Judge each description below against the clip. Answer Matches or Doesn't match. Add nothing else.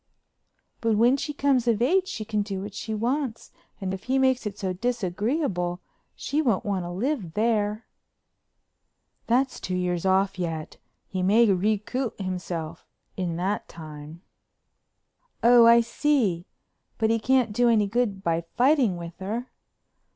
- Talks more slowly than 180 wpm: Matches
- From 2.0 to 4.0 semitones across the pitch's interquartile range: Doesn't match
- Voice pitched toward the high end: Matches